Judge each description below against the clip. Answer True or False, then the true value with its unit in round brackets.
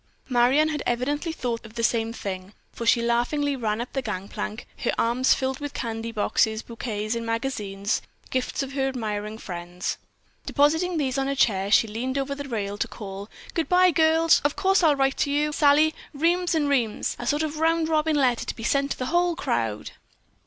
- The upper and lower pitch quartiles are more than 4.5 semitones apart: True (4.9 semitones)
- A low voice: False (255 Hz)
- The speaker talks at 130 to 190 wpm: False (200 wpm)